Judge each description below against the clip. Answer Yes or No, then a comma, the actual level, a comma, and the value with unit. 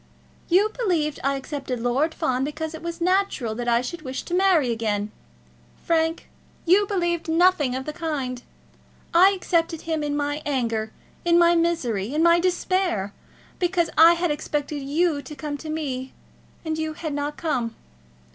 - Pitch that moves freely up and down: No, average, 4.3 semitones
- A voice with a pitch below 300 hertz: No, very high, 310 Hz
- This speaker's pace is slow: No, average, 165 wpm